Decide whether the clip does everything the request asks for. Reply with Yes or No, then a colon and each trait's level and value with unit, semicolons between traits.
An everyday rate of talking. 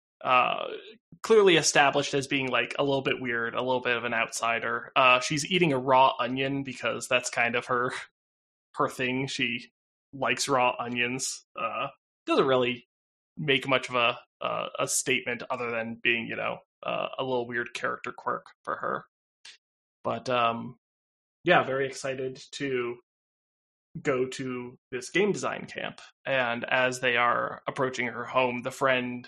Yes: average, 160 wpm